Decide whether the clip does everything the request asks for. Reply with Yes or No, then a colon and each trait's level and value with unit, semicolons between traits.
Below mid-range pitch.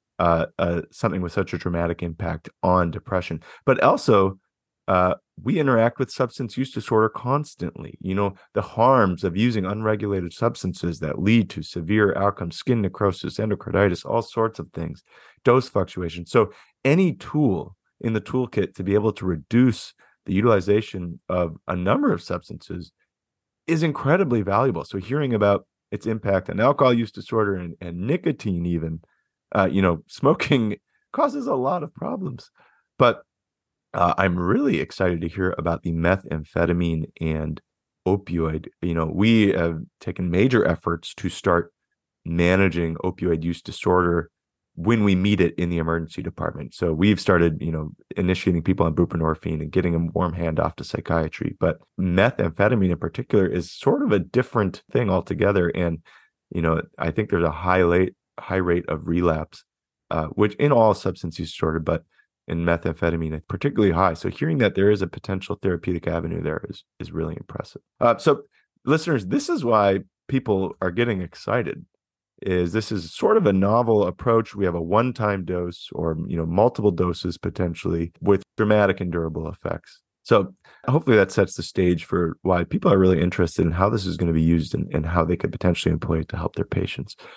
Yes: very low, 95 Hz